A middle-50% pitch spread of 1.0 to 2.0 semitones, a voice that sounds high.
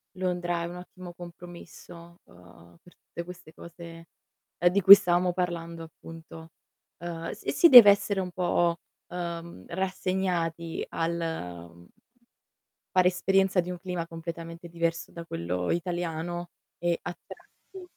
No: narrow, 1.4 semitones; medium, 170 Hz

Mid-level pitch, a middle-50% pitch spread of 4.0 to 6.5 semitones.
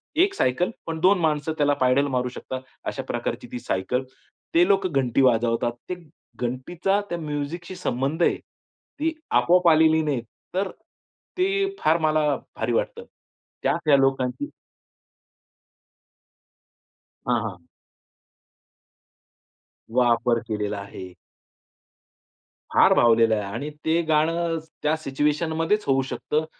Yes: medium, 150 Hz; average, 5.3 semitones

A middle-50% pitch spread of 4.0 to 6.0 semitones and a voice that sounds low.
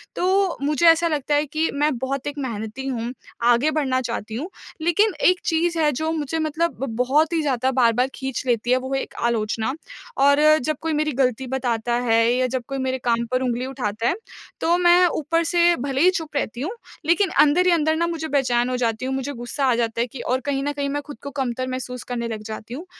No: average, 4.4 semitones; very high, 270 Hz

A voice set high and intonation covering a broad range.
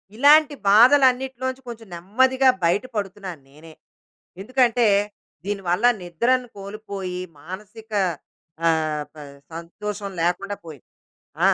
Yes: high, 205 Hz; wide, 5.9 semitones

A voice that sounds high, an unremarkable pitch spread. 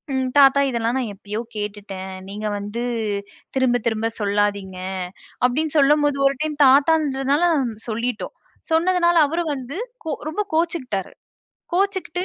No: very high, 260 Hz; wide, 6.7 semitones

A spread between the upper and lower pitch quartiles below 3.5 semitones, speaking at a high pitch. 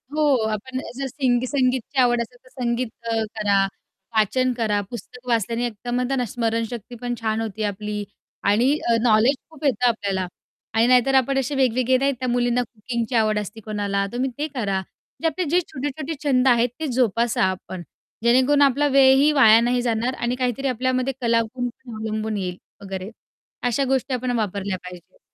Yes: average, 3.1 semitones; high, 240 Hz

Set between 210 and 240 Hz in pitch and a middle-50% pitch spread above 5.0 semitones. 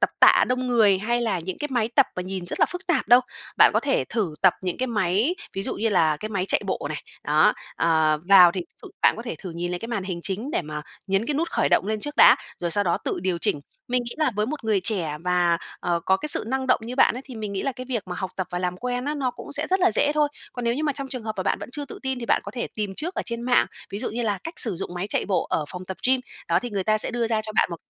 Yes: high, 215 Hz; wide, 5.4 semitones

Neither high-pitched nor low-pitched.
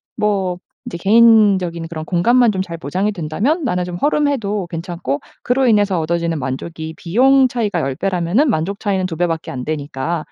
Yes: medium, 180 Hz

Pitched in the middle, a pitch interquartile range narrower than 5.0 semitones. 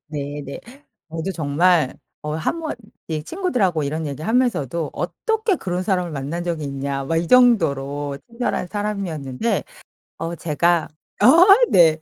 No: medium, 165 Hz; average, 5.3 semitones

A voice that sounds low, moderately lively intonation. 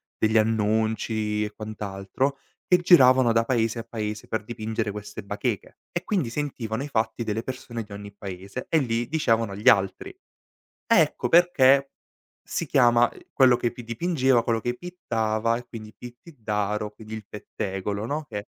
Yes: low, 115 Hz; average, 3.1 semitones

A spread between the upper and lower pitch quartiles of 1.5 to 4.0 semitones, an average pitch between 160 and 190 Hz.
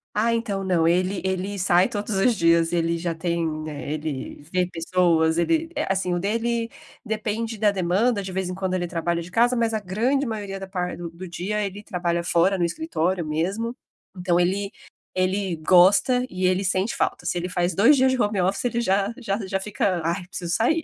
Yes: average, 3.4 semitones; medium, 185 Hz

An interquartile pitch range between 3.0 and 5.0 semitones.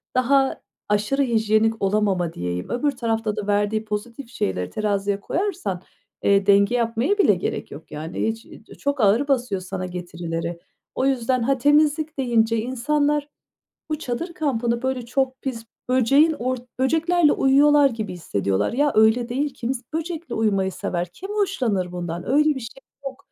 No: wide, 5.5 semitones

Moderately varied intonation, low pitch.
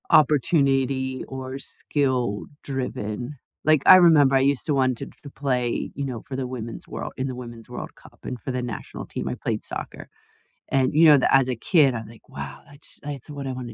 No: narrow, 2.2 semitones; low, 130 Hz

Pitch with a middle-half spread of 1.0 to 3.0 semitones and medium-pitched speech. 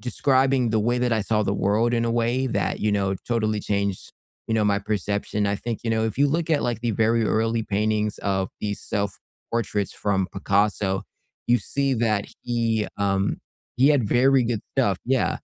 No: average, 2.7 semitones; low, 110 Hz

